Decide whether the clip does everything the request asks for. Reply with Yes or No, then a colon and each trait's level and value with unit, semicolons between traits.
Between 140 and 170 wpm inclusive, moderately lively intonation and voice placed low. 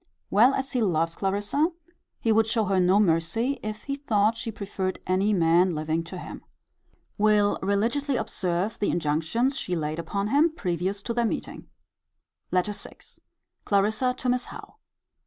No: average, 155 wpm; average, 4.4 semitones; high, 205 Hz